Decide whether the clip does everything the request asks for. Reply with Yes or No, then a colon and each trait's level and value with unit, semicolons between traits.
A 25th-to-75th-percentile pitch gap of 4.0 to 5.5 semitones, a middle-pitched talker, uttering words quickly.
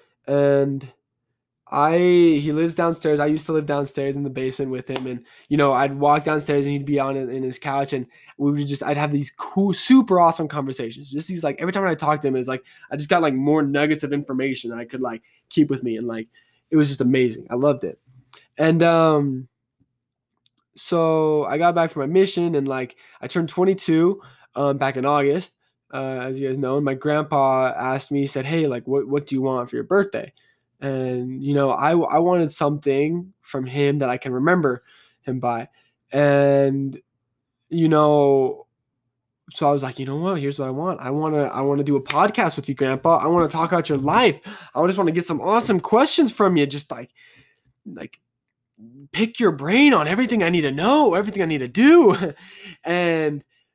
No: average, 3.6 semitones; medium, 145 Hz; fast, 210 wpm